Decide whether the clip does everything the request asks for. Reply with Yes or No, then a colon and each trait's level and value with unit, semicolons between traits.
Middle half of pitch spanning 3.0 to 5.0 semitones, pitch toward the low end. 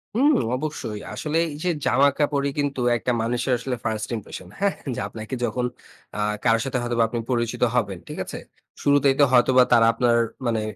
Yes: average, 3.5 semitones; low, 125 Hz